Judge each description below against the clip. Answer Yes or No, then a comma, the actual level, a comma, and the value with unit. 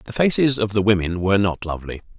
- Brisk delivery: Yes, fast, 220 wpm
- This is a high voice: No, low, 100 Hz